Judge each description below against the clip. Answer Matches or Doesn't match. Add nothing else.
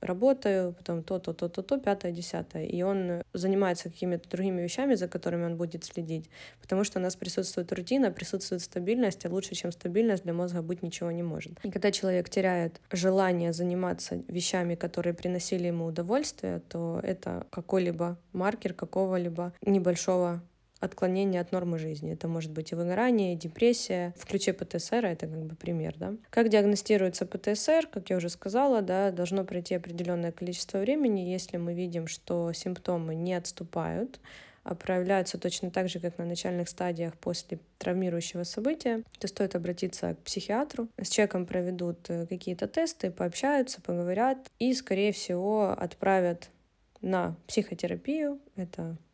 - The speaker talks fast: Doesn't match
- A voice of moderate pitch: Matches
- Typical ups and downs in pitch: Doesn't match